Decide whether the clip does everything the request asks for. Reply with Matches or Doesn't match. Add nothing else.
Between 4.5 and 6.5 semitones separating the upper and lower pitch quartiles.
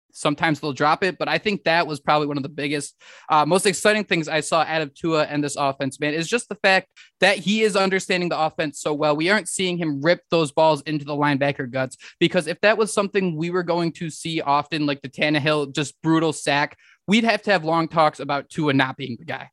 Doesn't match